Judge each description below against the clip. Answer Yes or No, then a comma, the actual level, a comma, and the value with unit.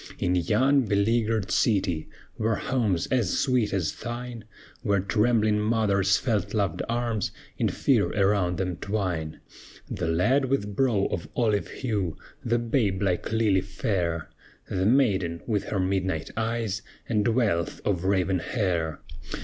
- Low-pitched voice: Yes, low, 100 Hz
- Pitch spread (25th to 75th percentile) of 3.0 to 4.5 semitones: Yes, average, 3.7 semitones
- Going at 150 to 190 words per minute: No, slow, 135 wpm